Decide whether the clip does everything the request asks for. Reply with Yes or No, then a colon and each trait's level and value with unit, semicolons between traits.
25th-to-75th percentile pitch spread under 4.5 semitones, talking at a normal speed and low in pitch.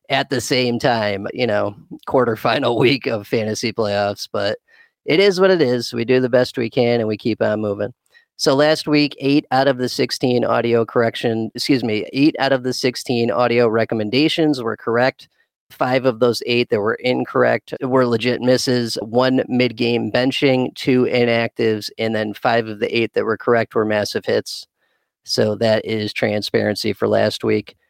Yes: average, 3.0 semitones; average, 180 wpm; low, 120 Hz